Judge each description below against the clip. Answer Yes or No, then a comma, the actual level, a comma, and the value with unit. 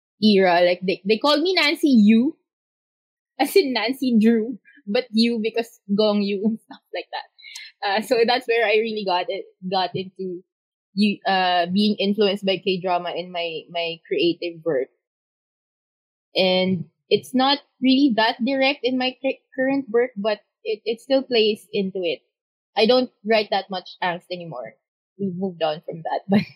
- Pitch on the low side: No, high, 215 Hz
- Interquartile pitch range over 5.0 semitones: Yes, wide, 5.6 semitones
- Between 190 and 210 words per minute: No, average, 165 wpm